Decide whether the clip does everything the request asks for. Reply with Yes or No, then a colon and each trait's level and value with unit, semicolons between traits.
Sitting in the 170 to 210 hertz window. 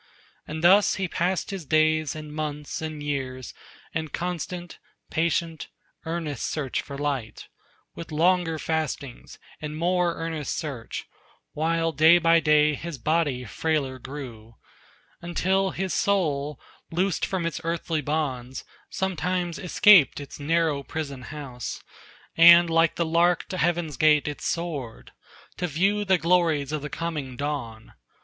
No: medium, 160 Hz